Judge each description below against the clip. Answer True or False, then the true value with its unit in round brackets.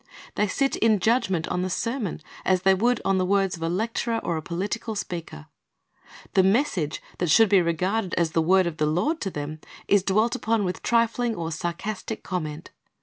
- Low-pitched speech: False (190 Hz)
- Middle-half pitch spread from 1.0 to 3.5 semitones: False (4.6 semitones)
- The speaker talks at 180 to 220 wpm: True (195 wpm)